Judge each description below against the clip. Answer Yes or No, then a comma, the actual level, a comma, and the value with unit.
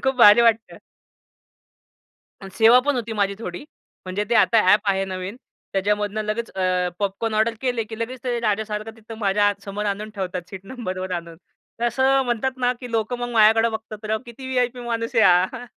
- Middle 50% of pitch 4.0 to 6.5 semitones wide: No, average, 2.9 semitones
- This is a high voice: Yes, high, 220 Hz